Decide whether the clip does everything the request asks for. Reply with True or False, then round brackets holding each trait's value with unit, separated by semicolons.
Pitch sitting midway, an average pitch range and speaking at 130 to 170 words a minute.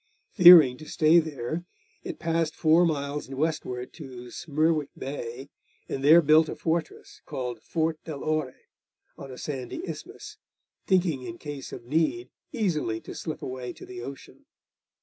True (155 Hz; 3.7 semitones; 150 wpm)